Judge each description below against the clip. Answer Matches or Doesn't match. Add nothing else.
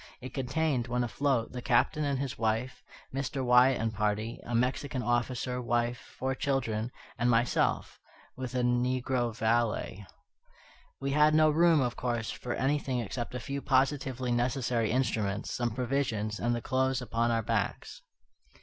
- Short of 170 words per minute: Matches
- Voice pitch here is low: Matches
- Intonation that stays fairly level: Matches